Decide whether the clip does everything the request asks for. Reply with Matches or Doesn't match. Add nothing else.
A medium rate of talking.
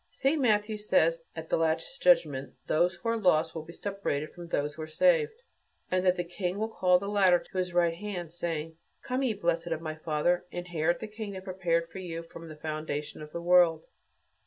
Doesn't match